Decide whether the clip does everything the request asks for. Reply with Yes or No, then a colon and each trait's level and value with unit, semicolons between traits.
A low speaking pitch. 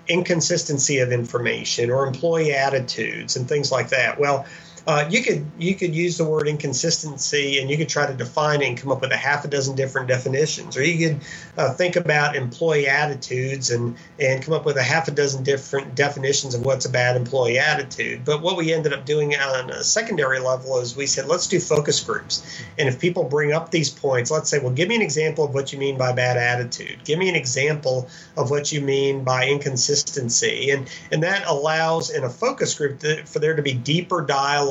No: medium, 145 Hz